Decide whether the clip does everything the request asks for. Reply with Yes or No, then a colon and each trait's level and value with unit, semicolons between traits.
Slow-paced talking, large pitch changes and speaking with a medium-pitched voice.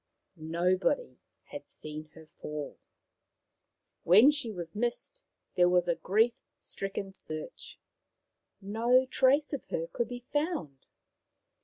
No: slow, 115 wpm; wide, 6.7 semitones; high, 195 Hz